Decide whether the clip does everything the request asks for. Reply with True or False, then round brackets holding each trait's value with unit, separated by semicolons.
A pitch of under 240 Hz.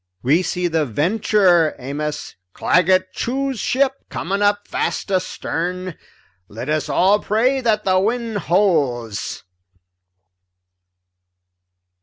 True (185 Hz)